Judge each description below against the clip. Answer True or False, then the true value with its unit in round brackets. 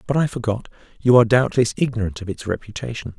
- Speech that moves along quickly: False (190 wpm)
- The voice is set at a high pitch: False (115 Hz)